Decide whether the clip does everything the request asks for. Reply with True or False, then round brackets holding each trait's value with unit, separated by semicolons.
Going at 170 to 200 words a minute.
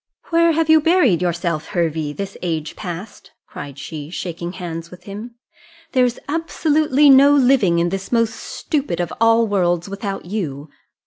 False (150 wpm)